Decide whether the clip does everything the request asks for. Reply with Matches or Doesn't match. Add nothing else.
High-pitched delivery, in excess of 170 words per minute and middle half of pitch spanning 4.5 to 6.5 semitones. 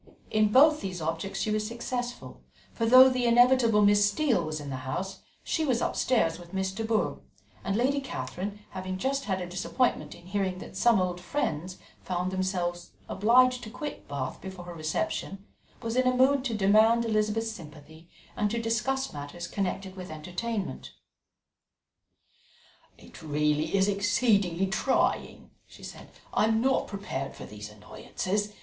Doesn't match